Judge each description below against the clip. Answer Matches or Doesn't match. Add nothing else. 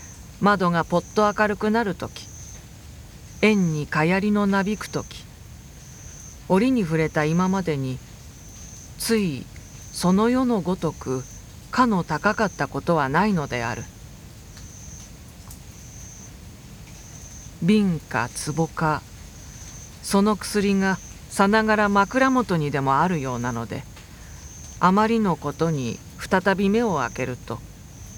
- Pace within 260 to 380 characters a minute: Doesn't match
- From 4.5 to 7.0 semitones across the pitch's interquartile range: Doesn't match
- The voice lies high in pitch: Doesn't match